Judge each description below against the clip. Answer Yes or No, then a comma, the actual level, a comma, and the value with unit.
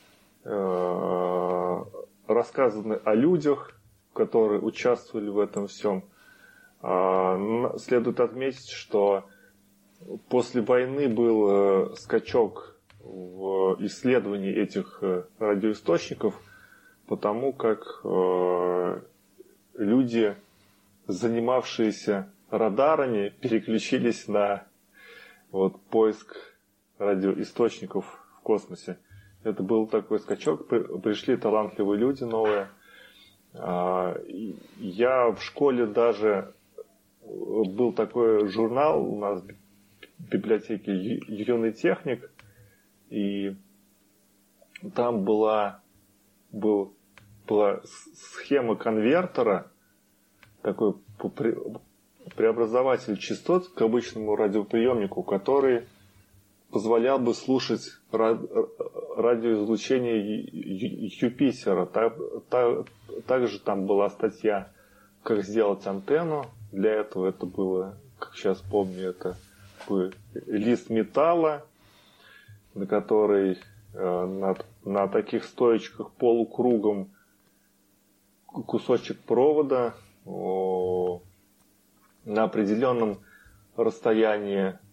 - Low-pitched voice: Yes, low, 105 Hz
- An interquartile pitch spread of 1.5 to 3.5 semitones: Yes, average, 2.7 semitones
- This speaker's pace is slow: Yes, slow, 70 wpm